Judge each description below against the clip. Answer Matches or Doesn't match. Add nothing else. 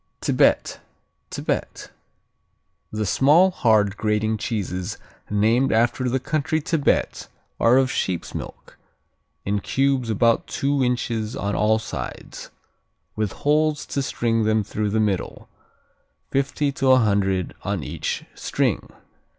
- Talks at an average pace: Doesn't match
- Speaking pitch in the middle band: Doesn't match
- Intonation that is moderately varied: Matches